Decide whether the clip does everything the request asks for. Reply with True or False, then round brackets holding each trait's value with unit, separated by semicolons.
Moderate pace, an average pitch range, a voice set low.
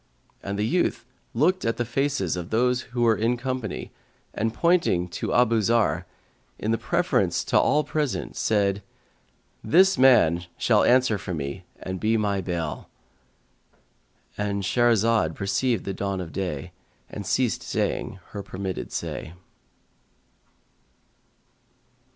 False (125 wpm; 4.3 semitones; 110 Hz)